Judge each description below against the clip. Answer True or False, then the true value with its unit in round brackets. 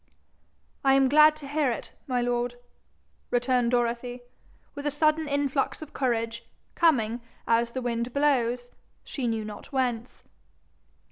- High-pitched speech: True (250 Hz)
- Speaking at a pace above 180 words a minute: False (135 wpm)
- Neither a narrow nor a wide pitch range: True (3.2 semitones)